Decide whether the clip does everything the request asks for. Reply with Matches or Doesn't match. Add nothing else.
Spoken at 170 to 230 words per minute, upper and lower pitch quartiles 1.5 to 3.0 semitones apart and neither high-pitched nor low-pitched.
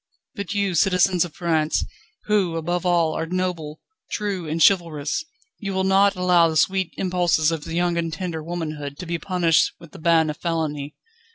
Matches